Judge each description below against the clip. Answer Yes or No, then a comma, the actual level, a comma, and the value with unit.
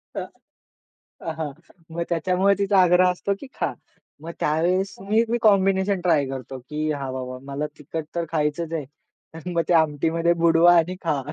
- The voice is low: No, medium, 165 Hz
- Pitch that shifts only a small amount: No, average, 3.3 semitones